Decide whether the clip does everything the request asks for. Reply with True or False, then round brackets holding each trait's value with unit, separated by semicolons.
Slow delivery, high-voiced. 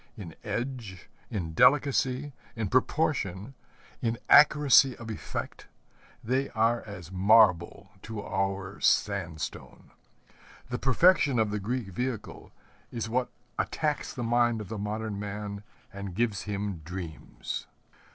False (120 wpm; 110 Hz)